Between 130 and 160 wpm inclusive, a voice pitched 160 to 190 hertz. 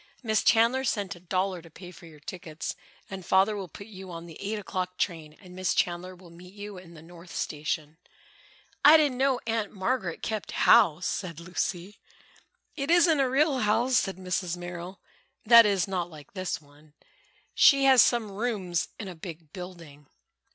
No: average, 180 wpm; medium, 185 Hz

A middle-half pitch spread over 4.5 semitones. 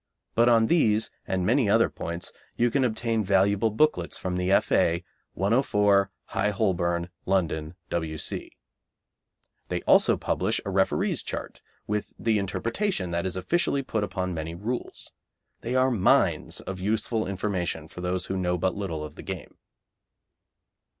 No: average, 4.0 semitones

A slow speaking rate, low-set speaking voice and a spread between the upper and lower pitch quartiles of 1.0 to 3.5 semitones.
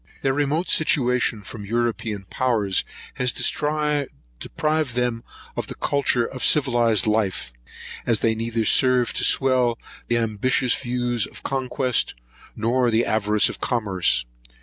Yes: slow, 125 wpm; low, 120 Hz; average, 2.8 semitones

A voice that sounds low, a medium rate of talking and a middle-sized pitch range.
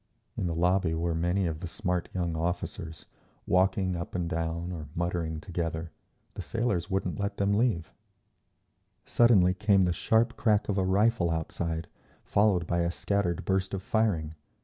Yes: very low, 90 Hz; average, 160 wpm; average, 3.0 semitones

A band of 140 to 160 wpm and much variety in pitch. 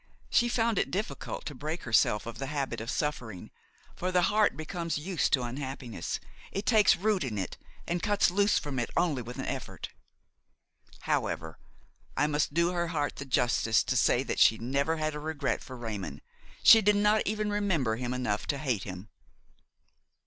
No: average, 180 wpm; wide, 7.0 semitones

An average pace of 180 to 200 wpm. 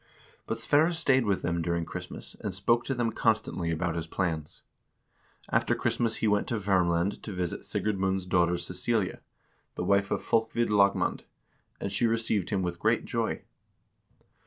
No: average, 160 wpm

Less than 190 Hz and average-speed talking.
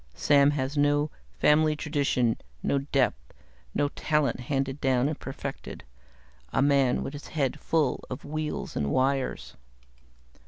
No: medium, 140 Hz; slow, 130 wpm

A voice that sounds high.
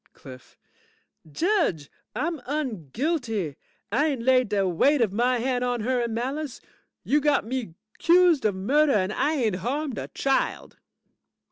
Yes: very high, 250 Hz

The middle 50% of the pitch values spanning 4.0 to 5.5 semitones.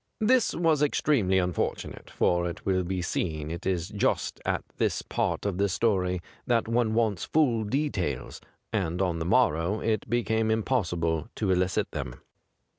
Yes: average, 4.5 semitones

